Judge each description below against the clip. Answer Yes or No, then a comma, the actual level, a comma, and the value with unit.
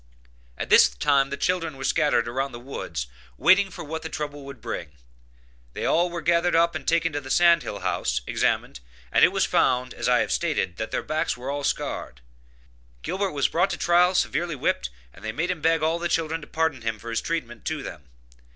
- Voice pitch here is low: No, medium, 150 Hz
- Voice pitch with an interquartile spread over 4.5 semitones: Yes, average, 5.2 semitones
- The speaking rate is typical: No, fast, 220 wpm